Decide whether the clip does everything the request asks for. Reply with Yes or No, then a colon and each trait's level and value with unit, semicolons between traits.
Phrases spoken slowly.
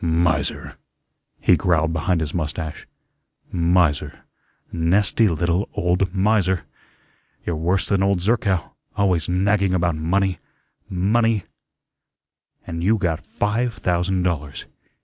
Yes: slow, 110 wpm